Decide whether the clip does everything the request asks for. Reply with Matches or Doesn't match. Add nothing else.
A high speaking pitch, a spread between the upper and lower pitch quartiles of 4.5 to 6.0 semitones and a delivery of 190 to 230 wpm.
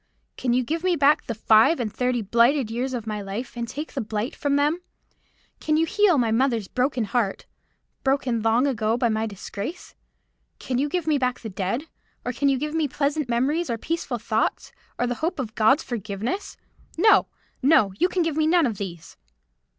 Matches